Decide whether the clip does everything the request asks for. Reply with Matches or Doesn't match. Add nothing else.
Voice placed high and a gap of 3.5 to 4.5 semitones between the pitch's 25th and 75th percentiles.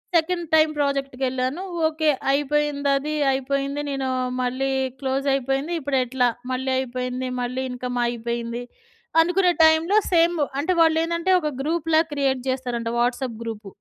Matches